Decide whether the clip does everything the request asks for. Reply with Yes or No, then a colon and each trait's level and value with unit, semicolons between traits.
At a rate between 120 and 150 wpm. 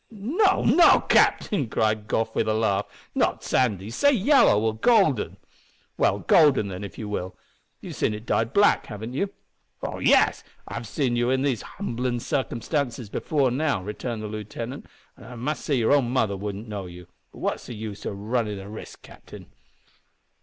No: average, 175 wpm